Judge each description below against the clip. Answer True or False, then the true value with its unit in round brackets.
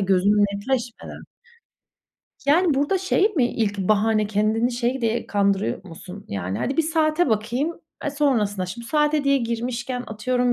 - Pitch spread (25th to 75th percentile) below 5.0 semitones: False (5.3 semitones)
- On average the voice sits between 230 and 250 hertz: True (235 Hz)